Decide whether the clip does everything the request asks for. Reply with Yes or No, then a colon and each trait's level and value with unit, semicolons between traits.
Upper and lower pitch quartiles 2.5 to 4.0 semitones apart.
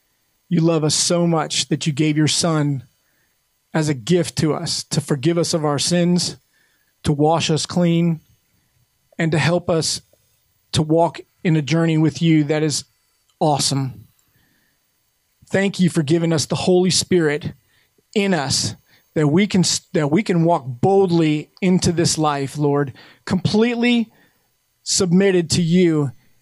Yes: average, 2.9 semitones